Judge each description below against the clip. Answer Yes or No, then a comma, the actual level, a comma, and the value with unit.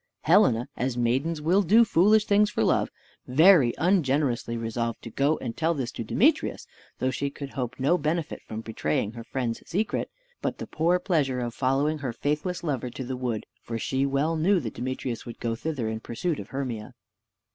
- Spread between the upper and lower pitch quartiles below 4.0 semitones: No, wide, 5.6 semitones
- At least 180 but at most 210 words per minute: Yes, average, 190 wpm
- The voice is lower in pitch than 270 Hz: Yes, low, 135 Hz